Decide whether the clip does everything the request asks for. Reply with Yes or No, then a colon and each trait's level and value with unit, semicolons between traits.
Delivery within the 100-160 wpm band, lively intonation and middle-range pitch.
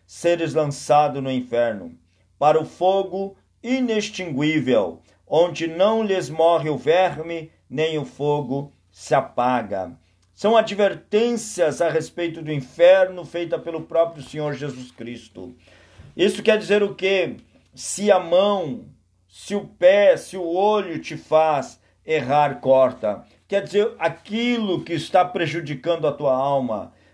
Yes: average, 130 wpm; wide, 5.8 semitones; medium, 160 Hz